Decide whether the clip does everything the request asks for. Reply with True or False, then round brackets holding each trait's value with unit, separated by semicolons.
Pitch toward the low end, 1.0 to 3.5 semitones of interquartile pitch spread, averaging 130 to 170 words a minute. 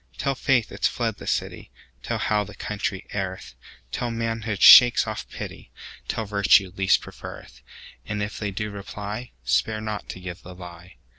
True (105 Hz; 2.8 semitones; 140 wpm)